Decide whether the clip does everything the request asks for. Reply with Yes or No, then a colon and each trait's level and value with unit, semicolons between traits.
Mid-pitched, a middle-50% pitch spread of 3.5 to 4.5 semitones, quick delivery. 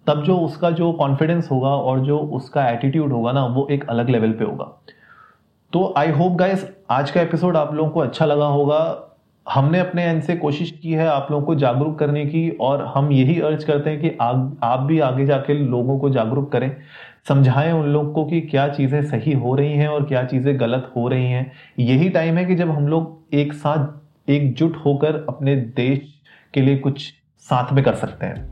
No: medium, 145 Hz; narrow, 2.6 semitones; fast, 210 wpm